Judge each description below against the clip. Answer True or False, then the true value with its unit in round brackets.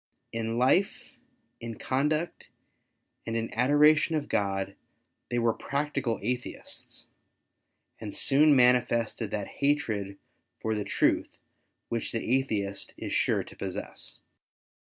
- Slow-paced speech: True (115 wpm)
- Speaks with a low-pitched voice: True (120 Hz)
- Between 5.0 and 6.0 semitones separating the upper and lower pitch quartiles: False (4.3 semitones)